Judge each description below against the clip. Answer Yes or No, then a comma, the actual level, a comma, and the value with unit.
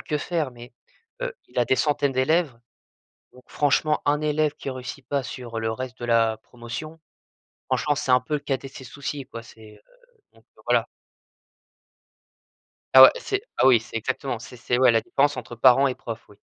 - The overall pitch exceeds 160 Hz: No, low, 130 Hz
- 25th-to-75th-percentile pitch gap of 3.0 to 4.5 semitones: Yes, average, 3.5 semitones